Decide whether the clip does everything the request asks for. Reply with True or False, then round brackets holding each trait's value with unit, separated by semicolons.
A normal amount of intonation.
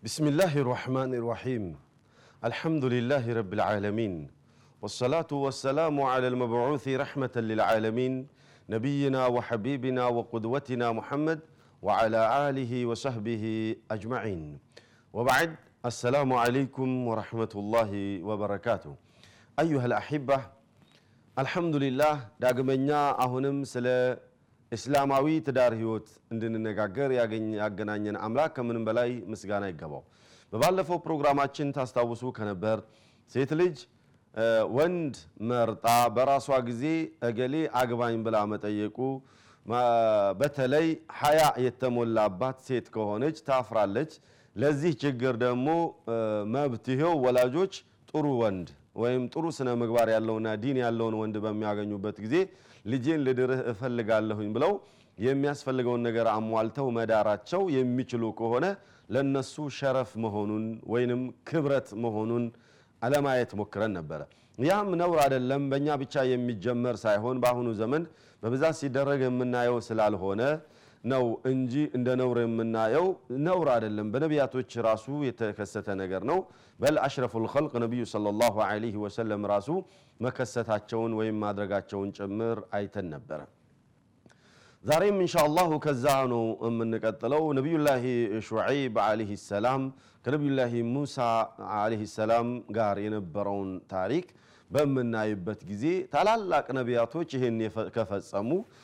True (3.6 semitones)